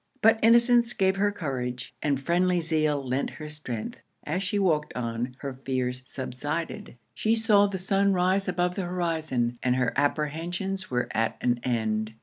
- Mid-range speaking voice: Yes, medium, 155 Hz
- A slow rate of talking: No, average, 160 wpm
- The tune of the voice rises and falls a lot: Yes, wide, 7.0 semitones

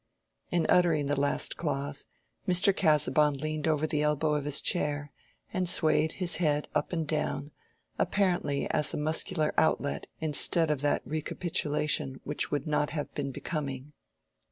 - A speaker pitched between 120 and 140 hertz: No, medium, 150 Hz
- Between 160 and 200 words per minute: No, average, 150 wpm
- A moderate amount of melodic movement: No, narrow, 1.7 semitones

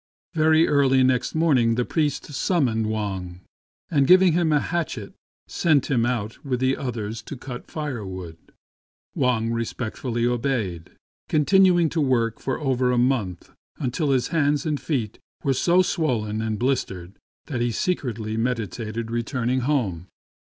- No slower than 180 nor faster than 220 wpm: No, average, 145 wpm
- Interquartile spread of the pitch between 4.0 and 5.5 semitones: Yes, average, 4.6 semitones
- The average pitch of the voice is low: Yes, low, 125 Hz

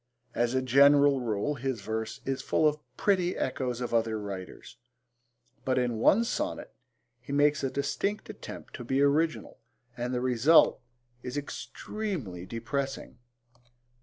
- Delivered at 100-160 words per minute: Yes, slow, 135 wpm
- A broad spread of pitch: No, average, 3.5 semitones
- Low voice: Yes, low, 130 Hz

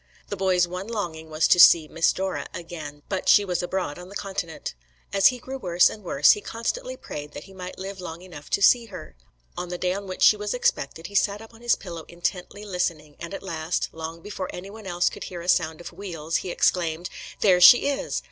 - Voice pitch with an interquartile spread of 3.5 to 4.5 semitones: No, average, 3.1 semitones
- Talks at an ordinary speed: No, fast, 225 wpm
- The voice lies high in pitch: No, medium, 180 Hz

